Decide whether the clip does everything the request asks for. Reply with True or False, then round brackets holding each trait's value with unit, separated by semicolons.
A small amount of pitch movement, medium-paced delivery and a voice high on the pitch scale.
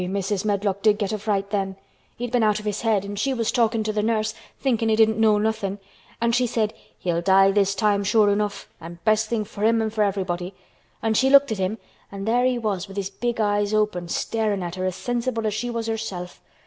False (2.2 semitones; 240 wpm; 210 Hz)